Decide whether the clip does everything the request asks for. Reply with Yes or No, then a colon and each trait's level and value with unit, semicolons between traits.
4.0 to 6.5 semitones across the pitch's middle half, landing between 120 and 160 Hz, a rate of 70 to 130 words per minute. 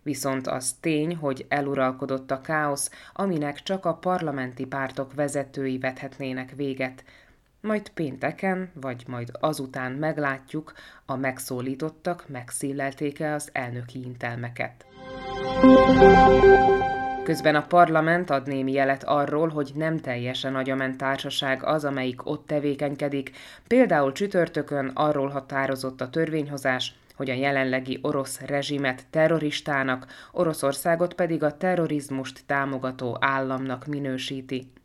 No: narrow, 2.5 semitones; medium, 140 Hz; slow, 105 wpm